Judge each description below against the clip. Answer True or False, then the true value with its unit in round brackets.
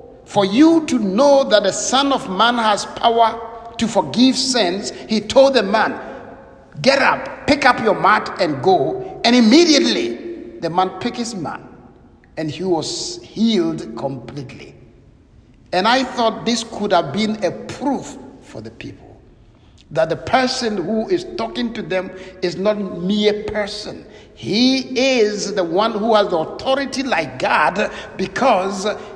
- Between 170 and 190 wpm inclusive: False (150 wpm)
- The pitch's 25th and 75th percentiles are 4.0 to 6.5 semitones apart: True (5.2 semitones)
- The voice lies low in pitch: False (220 Hz)